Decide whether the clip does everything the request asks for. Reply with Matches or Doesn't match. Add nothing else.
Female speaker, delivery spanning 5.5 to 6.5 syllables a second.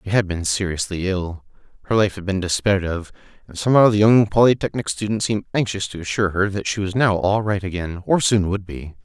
Doesn't match